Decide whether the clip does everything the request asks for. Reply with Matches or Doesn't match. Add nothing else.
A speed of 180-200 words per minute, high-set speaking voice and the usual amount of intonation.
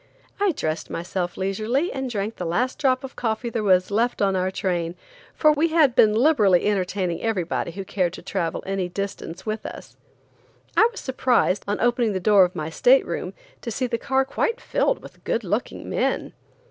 Doesn't match